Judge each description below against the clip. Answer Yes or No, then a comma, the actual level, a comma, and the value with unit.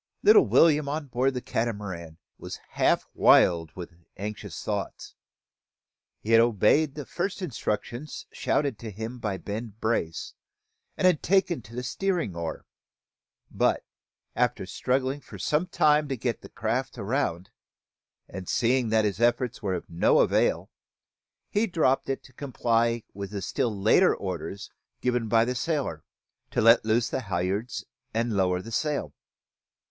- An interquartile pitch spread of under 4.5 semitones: No, average, 5.2 semitones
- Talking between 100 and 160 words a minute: Yes, average, 145 wpm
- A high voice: No, low, 115 Hz